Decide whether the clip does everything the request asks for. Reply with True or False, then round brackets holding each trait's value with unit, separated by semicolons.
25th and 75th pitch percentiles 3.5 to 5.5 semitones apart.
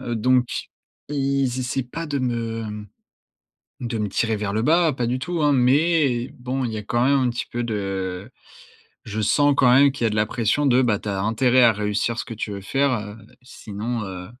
True (3.8 semitones)